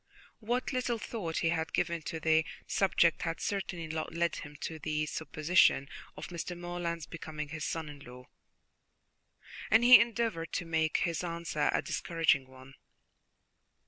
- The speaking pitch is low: No, medium, 165 Hz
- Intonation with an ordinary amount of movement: No, narrow, 2.2 semitones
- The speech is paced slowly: No, average, 150 wpm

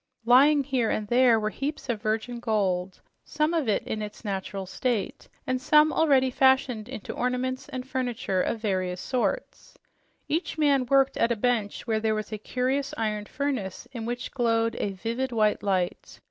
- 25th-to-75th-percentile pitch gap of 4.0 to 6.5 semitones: No, average, 3.6 semitones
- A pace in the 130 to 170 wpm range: Yes, average, 165 wpm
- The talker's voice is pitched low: No, high, 240 Hz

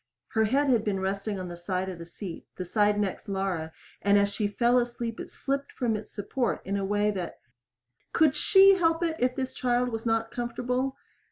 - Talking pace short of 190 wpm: No, fast, 205 wpm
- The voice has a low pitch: No, high, 220 Hz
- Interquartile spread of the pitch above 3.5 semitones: Yes, average, 4.2 semitones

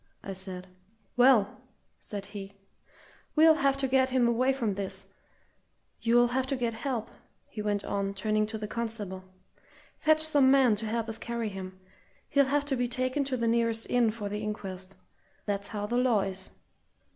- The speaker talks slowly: No, average, 175 wpm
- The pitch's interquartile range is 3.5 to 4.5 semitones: Yes, average, 4.1 semitones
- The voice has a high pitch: Yes, high, 225 Hz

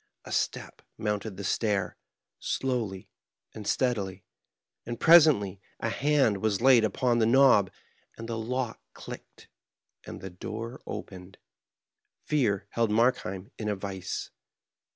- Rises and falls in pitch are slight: No, average, 4.0 semitones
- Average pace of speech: No, slow, 125 wpm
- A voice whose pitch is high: No, low, 110 Hz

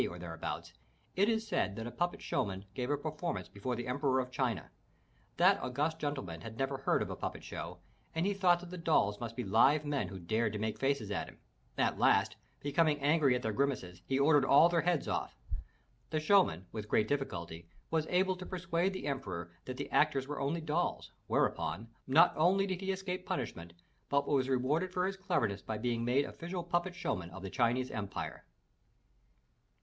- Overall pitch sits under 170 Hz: Yes, medium, 140 Hz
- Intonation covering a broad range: Yes, wide, 7.4 semitones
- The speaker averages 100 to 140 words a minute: No, average, 200 wpm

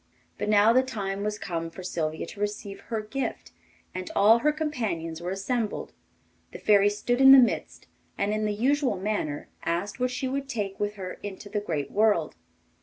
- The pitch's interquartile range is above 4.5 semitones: No, average, 4.0 semitones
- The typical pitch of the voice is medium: No, high, 210 Hz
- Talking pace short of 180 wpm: No, average, 185 wpm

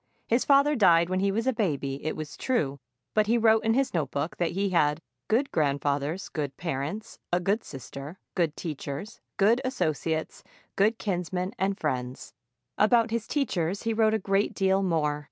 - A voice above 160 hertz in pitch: Yes, medium, 185 Hz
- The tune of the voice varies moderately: No, wide, 6.3 semitones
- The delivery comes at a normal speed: Yes, average, 170 wpm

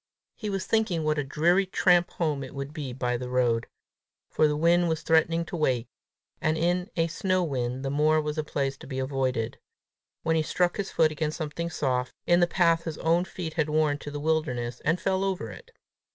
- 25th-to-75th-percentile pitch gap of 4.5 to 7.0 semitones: No, average, 4.0 semitones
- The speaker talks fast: Yes, fast, 210 wpm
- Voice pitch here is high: No, medium, 155 Hz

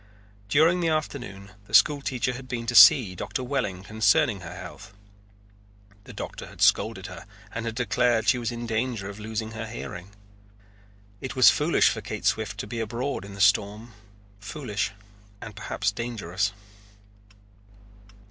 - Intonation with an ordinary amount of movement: Yes, average, 3.7 semitones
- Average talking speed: Yes, average, 155 wpm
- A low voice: Yes, low, 115 Hz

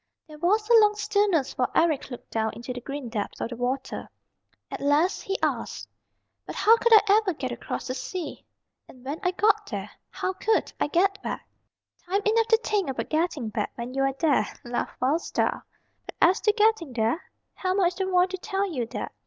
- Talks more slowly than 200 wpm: No, fast, 205 wpm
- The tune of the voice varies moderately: No, wide, 7.5 semitones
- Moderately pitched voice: No, very high, 340 Hz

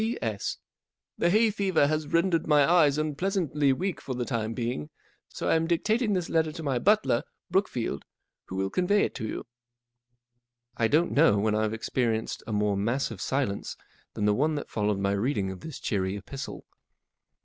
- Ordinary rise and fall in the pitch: No, wide, 7.7 semitones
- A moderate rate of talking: Yes, average, 175 wpm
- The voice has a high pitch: No, low, 135 Hz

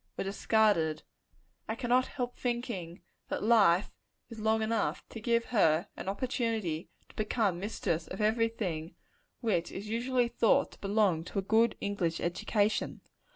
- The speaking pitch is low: No, high, 215 Hz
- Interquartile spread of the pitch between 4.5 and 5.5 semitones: No, average, 4.0 semitones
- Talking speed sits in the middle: Yes, average, 150 wpm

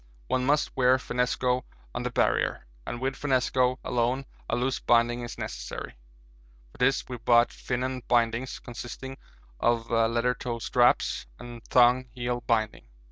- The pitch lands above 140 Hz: No, low, 125 Hz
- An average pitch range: No, narrow, 1.3 semitones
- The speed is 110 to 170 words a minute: Yes, average, 140 wpm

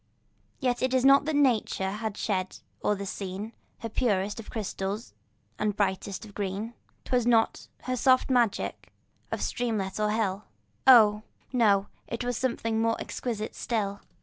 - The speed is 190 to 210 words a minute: No, average, 150 wpm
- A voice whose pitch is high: Yes, high, 220 Hz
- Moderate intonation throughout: Yes, average, 3.3 semitones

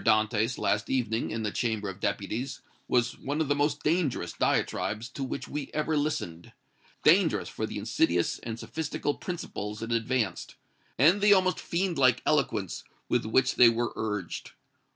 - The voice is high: No, low, 120 Hz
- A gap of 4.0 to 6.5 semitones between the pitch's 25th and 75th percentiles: Yes, average, 5.2 semitones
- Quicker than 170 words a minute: No, average, 160 wpm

